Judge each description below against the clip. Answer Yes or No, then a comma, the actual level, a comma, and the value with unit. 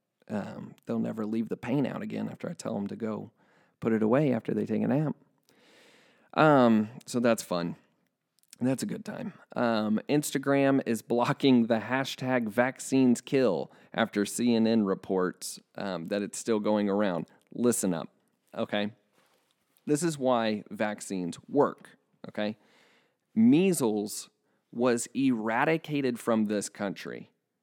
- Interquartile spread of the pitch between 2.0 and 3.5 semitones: No, average, 4.3 semitones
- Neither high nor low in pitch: No, low, 115 Hz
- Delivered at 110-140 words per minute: Yes, slow, 135 wpm